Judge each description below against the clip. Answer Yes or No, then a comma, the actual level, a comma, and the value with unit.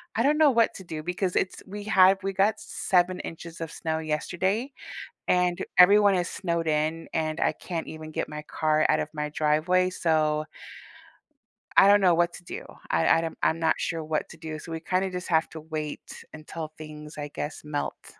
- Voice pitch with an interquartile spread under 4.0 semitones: Yes, average, 3.0 semitones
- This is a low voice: No, medium, 165 Hz